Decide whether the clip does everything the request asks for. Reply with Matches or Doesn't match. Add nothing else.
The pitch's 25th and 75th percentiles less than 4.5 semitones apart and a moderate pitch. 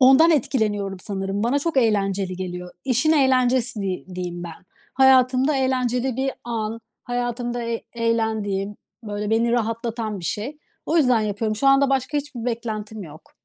Doesn't match